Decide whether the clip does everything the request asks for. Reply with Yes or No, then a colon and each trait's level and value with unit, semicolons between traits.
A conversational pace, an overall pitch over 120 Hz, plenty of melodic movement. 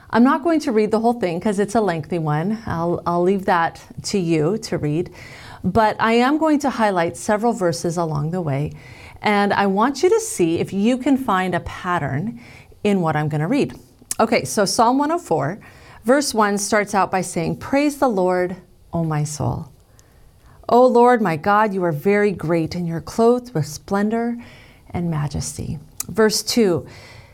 Yes: average, 180 wpm; medium, 185 Hz; wide, 6.1 semitones